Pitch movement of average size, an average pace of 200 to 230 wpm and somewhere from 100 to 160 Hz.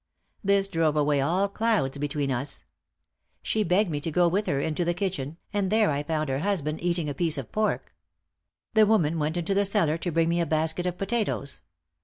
No: average, 4.8 semitones; fast, 205 wpm; medium, 170 Hz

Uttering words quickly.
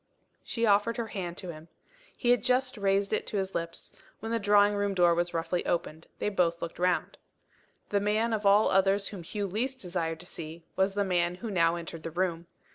Yes: fast, 210 wpm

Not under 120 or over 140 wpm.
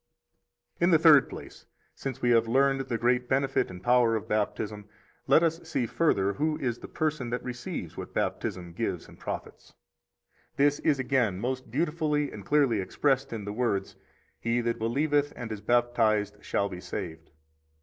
No: average, 175 wpm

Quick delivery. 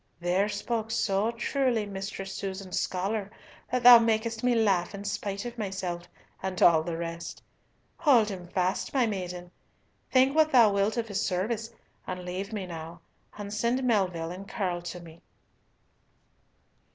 No: average, 150 wpm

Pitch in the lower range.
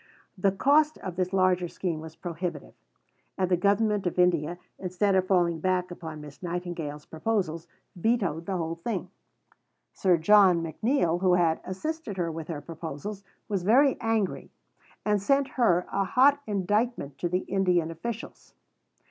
No: medium, 180 Hz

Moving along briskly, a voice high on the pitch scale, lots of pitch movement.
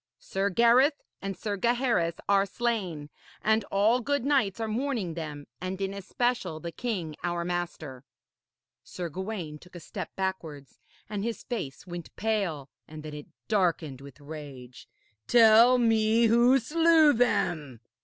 No: average, 145 wpm; high, 195 Hz; wide, 6.5 semitones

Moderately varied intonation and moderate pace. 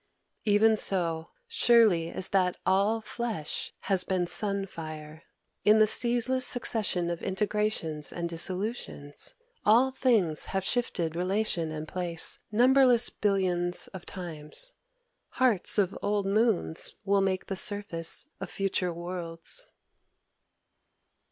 No: average, 4.2 semitones; slow, 115 wpm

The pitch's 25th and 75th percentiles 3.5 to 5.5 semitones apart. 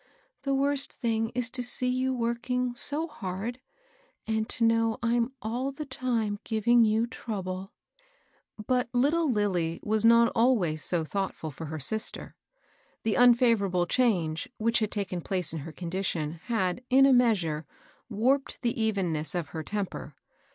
Yes: average, 5.0 semitones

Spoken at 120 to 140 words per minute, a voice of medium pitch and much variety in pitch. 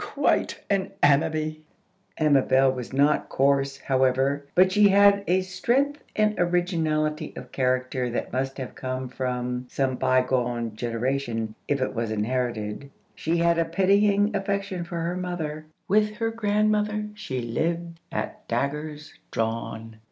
Yes: slow, 135 wpm; medium, 150 Hz; wide, 6.5 semitones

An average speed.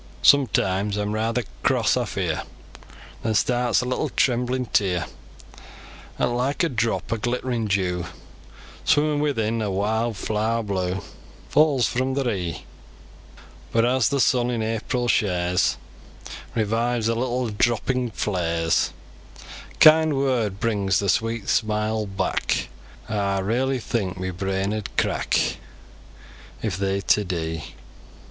No: slow, 125 wpm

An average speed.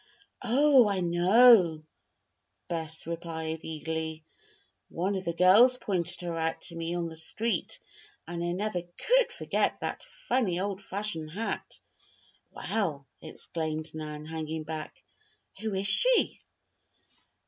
No: slow, 125 wpm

